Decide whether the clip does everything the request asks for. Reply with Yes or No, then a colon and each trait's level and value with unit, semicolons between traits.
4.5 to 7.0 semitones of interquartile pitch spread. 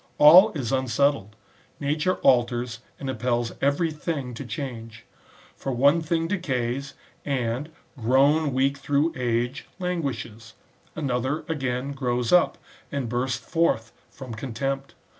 No: average, 3.5 semitones